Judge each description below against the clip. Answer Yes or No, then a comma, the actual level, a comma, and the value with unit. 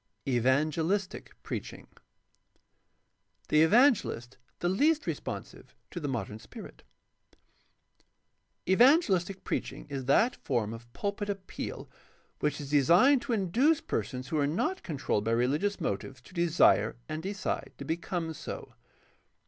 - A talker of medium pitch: Yes, medium, 165 Hz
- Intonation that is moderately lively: No, wide, 7.3 semitones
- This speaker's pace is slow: Yes, slow, 125 wpm